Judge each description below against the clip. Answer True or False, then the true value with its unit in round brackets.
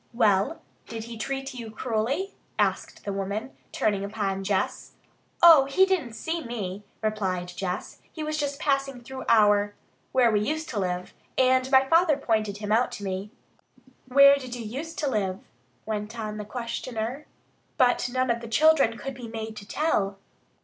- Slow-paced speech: False (170 wpm)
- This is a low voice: False (230 Hz)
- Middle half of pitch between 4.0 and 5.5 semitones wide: True (4.6 semitones)